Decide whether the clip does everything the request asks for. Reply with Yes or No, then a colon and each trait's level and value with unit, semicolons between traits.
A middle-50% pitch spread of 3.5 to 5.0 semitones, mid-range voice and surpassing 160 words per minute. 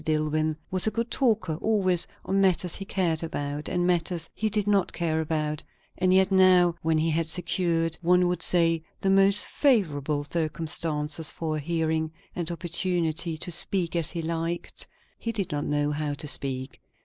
No: average, 2.8 semitones; medium, 165 Hz; average, 175 wpm